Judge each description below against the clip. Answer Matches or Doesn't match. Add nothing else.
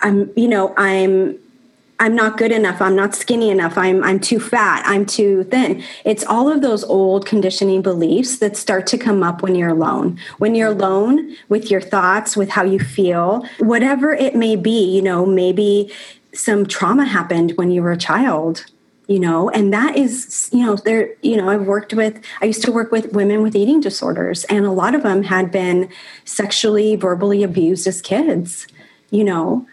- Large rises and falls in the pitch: Doesn't match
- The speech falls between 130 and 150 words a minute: Doesn't match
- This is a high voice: Matches